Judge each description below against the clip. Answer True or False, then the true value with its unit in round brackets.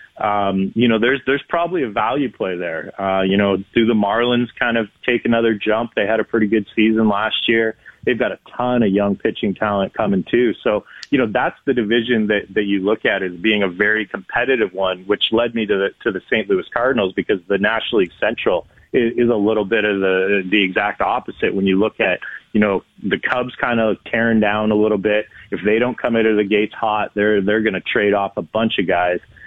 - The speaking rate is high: True (235 wpm)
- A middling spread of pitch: False (2.2 semitones)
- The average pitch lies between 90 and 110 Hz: True (105 Hz)